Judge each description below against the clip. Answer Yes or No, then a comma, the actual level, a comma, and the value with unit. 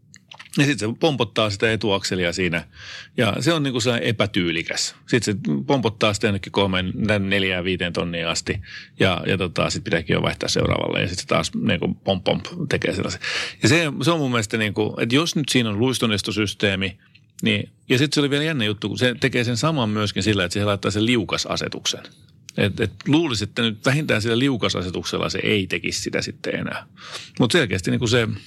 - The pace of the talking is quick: Yes, fast, 195 wpm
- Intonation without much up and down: No, average, 4.3 semitones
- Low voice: Yes, low, 110 Hz